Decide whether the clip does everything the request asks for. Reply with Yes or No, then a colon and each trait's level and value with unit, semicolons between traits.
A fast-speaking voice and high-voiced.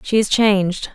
No: average, 190 wpm; high, 200 Hz